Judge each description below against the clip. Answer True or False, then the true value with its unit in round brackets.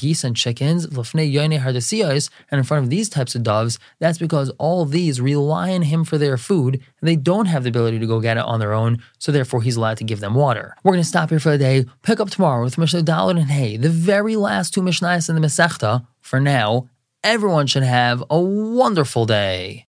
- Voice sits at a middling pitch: True (145 Hz)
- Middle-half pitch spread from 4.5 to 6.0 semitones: True (5.4 semitones)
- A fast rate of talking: True (225 wpm)